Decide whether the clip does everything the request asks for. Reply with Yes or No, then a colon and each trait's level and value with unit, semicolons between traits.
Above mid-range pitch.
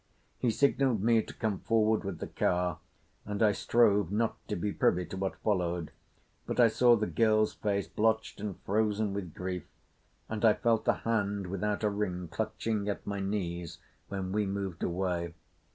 No: low, 100 Hz